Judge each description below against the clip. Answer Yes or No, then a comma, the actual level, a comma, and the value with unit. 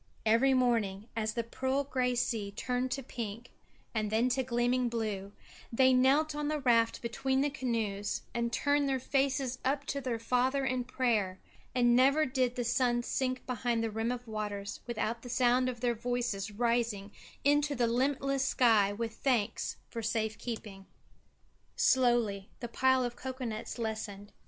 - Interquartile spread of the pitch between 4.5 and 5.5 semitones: No, average, 2.7 semitones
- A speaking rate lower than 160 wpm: No, average, 165 wpm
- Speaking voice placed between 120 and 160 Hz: No, high, 240 Hz